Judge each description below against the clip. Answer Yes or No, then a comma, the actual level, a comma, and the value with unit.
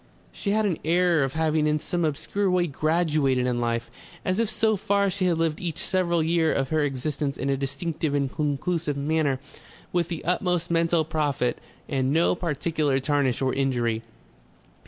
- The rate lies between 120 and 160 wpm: No, average, 175 wpm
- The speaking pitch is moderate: Yes, medium, 155 Hz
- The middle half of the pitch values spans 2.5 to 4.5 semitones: Yes, average, 4.0 semitones